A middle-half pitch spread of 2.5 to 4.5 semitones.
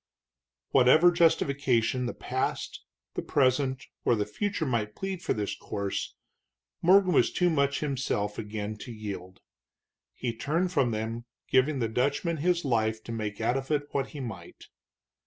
No: average, 5.1 semitones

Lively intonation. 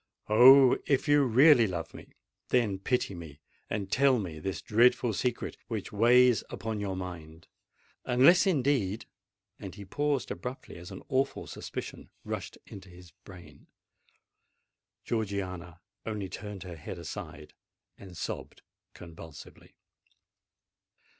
Yes: wide, 5.7 semitones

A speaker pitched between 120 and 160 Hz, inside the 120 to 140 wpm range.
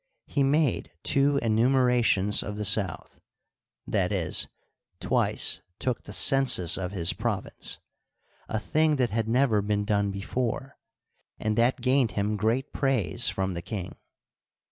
No: low, 110 Hz; slow, 135 wpm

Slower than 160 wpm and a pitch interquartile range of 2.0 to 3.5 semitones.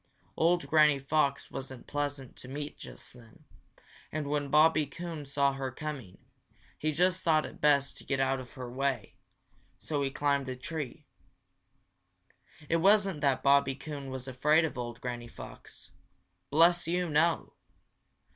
Yes: average, 150 wpm; average, 2.8 semitones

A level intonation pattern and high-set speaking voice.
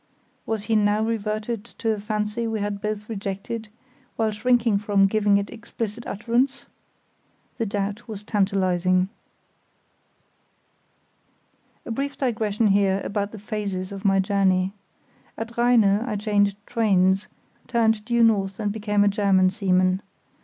Yes: narrow, 2.2 semitones; high, 210 Hz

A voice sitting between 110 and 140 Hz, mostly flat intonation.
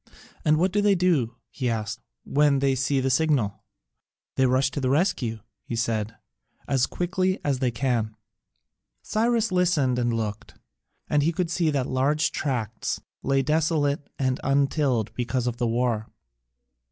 No: low, 135 Hz; average, 4.5 semitones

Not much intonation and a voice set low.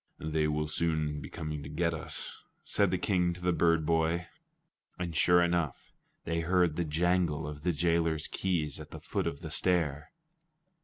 Yes: narrow, 2.3 semitones; very low, 80 Hz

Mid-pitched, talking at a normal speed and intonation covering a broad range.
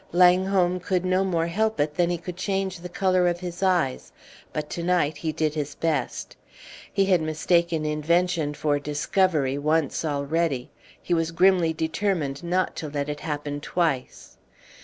No: medium, 170 Hz; average, 160 wpm; average, 3.2 semitones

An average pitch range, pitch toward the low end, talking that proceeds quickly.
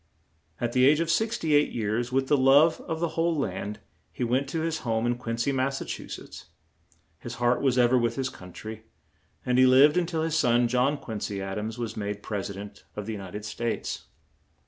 Yes: average, 4.8 semitones; low, 125 Hz; fast, 225 wpm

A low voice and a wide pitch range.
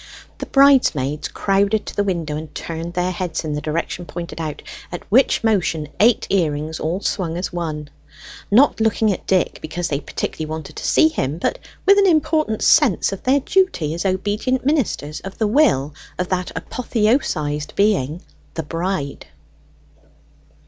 No: medium, 180 Hz; wide, 5.9 semitones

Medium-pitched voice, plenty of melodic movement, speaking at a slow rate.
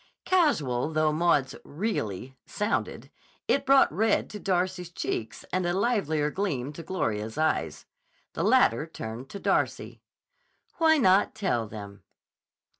Yes: medium, 160 Hz; wide, 8.0 semitones; slow, 125 wpm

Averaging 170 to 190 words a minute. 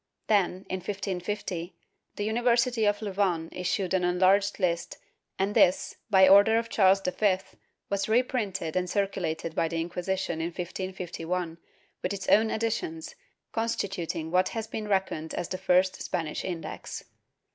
No: average, 145 wpm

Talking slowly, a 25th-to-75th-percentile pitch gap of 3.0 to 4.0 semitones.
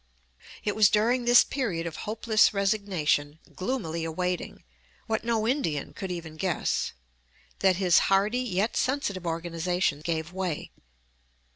No: slow, 125 wpm; average, 4.6 semitones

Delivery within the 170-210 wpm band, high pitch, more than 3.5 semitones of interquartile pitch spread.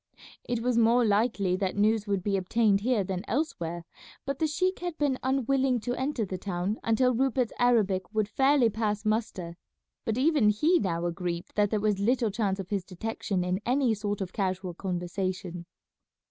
Yes: average, 175 wpm; high, 210 Hz; average, 4.6 semitones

